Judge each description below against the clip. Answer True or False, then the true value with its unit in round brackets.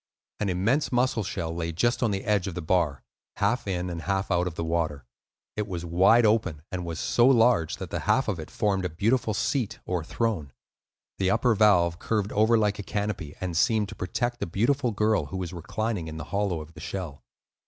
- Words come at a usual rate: False (215 wpm)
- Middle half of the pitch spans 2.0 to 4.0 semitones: False (4.5 semitones)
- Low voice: True (95 Hz)